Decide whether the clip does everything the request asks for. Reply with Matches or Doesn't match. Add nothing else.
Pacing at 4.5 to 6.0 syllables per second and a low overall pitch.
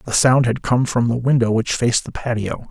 Matches